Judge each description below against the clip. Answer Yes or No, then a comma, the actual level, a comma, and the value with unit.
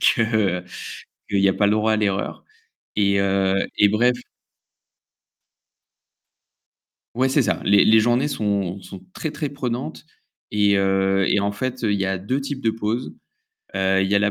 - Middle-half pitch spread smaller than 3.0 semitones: No, average, 3.4 semitones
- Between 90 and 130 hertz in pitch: Yes, low, 105 Hz